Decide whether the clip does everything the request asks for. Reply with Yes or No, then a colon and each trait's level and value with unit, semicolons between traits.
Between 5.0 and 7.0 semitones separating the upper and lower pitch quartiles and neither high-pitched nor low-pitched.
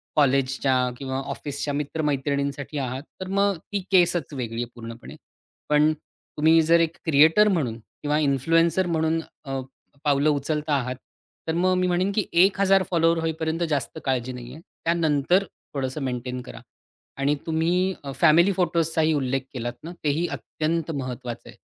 No: average, 3.7 semitones; medium, 150 Hz